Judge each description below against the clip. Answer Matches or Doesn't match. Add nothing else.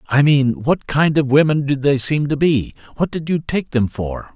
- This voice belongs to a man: Matches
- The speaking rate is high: Matches